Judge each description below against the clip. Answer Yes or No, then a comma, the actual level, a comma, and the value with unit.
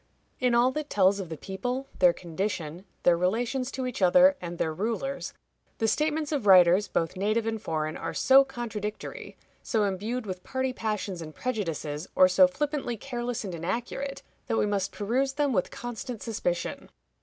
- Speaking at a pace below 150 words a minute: No, average, 170 wpm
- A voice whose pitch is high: Yes, high, 215 Hz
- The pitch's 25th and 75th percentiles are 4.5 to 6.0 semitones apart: Yes, wide, 5.6 semitones